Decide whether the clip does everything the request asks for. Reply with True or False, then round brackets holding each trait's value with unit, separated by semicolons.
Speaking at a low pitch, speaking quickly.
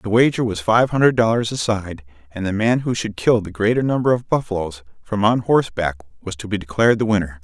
True (105 Hz; 225 wpm)